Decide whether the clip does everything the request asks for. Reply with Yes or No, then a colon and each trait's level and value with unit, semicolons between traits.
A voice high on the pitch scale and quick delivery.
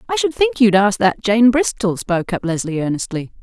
Yes: high, 210 Hz; fast, 210 wpm